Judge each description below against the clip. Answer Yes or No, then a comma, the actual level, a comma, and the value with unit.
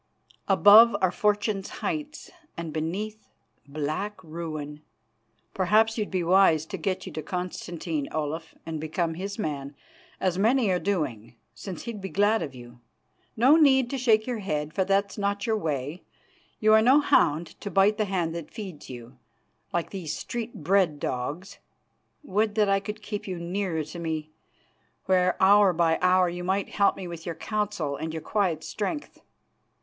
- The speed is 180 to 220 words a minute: No, average, 165 wpm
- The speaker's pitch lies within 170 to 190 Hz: Yes, medium, 185 Hz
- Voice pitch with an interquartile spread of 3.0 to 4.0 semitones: No, average, 4.5 semitones